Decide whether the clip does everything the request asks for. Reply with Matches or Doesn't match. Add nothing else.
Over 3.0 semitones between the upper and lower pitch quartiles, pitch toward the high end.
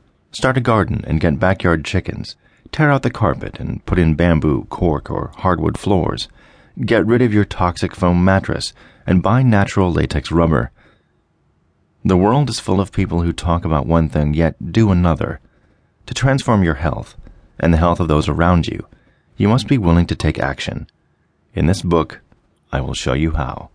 Doesn't match